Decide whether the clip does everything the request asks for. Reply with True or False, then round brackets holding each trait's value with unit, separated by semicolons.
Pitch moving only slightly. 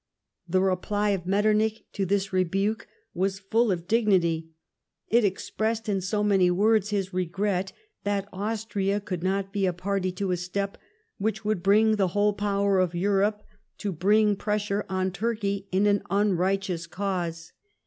True (1.9 semitones)